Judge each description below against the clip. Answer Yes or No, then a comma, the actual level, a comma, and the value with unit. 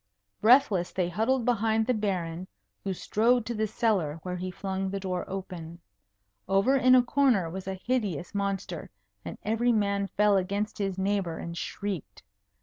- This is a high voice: Yes, high, 200 Hz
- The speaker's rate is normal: Yes, average, 160 wpm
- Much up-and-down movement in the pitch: No, average, 3.3 semitones